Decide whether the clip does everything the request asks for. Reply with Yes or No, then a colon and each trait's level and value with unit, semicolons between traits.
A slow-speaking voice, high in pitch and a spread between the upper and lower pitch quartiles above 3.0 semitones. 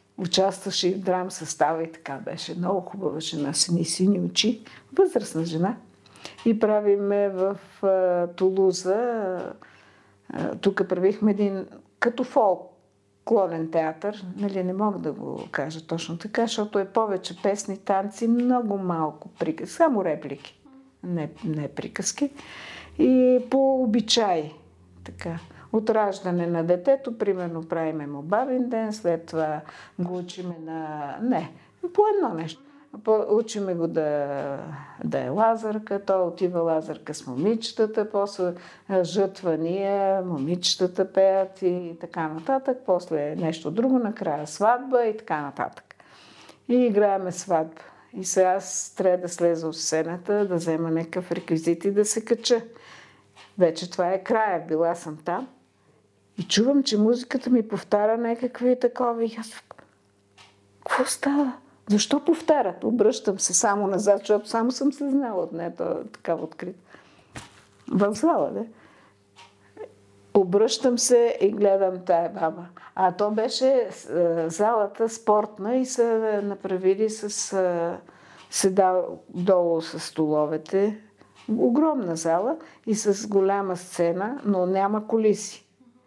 Yes: slow, 125 wpm; high, 195 Hz; average, 4.8 semitones